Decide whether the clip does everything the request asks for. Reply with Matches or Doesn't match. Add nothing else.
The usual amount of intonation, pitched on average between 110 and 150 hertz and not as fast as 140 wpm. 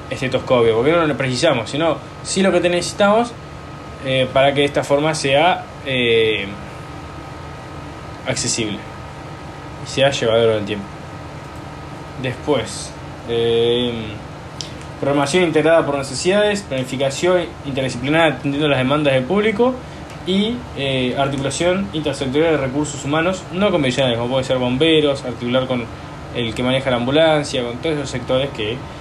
Matches